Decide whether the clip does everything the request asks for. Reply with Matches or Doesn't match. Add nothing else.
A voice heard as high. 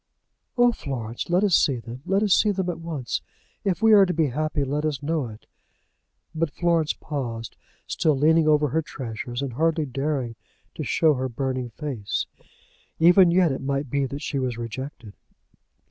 Doesn't match